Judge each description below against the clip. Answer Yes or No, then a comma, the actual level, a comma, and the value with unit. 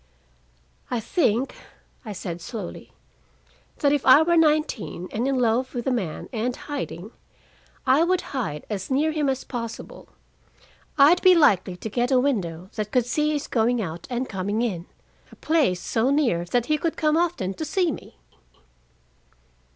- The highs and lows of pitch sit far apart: Yes, wide, 6.2 semitones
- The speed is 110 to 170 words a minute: Yes, average, 165 wpm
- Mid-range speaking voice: No, high, 245 Hz